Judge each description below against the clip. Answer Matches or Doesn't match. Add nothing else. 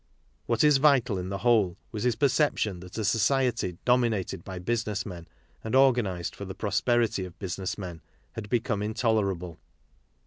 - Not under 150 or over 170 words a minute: Matches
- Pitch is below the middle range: Matches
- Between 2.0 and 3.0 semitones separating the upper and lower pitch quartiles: Doesn't match